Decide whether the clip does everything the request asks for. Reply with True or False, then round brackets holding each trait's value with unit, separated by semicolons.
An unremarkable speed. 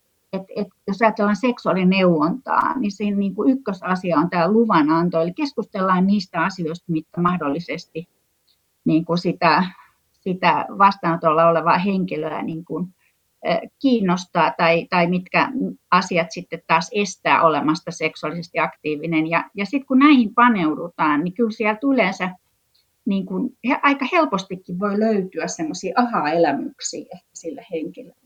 True (125 wpm)